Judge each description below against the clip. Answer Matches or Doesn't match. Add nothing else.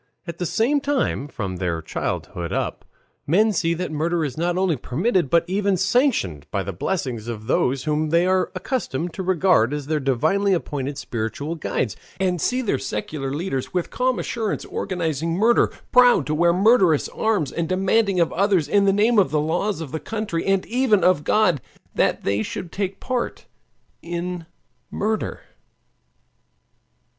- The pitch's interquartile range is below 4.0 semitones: Doesn't match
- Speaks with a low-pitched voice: Doesn't match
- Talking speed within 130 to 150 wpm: Doesn't match